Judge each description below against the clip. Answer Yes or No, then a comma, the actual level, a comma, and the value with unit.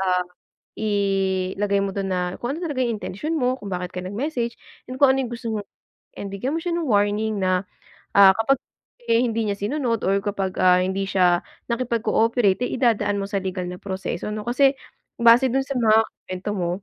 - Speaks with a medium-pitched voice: No, high, 205 Hz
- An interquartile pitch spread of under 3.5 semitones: No, average, 3.8 semitones